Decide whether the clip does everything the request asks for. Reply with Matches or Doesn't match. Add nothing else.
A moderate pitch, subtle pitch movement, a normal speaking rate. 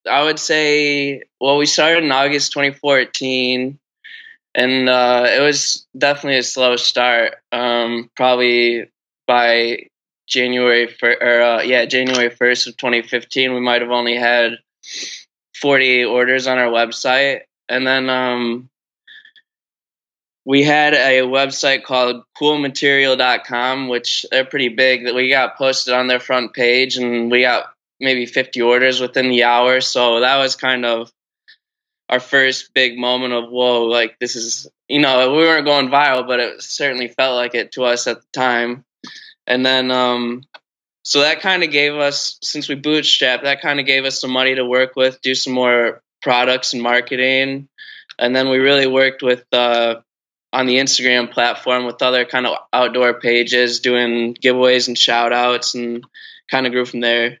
Doesn't match